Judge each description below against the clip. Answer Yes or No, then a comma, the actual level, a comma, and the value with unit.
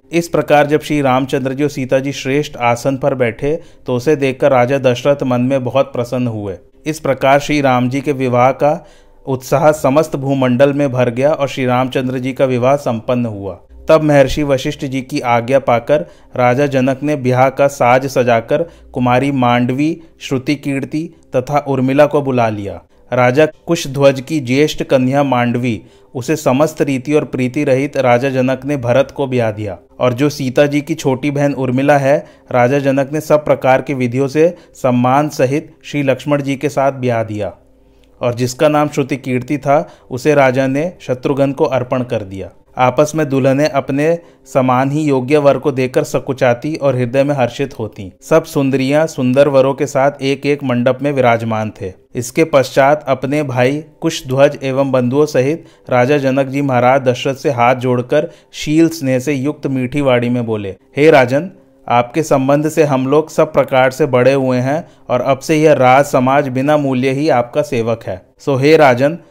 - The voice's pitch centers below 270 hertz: Yes, low, 135 Hz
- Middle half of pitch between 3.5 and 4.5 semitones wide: No, narrow, 2.6 semitones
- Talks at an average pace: Yes, average, 180 wpm